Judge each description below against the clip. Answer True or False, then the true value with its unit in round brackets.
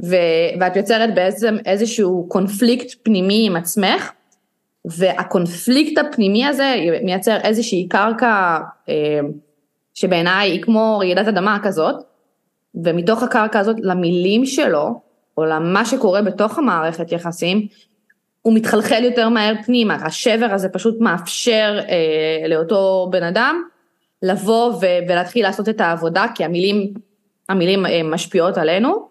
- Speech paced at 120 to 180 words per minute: False (110 wpm)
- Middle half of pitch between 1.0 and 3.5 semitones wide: False (4.2 semitones)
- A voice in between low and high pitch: False (200 Hz)